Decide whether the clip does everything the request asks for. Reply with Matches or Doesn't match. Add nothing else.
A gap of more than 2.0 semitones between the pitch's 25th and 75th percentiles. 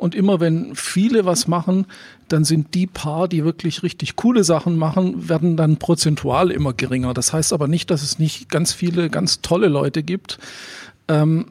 Matches